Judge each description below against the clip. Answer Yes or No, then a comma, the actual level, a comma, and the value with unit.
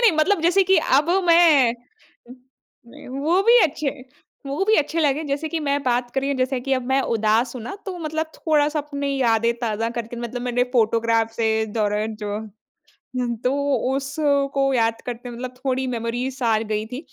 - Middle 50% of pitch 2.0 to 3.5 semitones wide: No, average, 4.2 semitones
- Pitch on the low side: No, very high, 260 Hz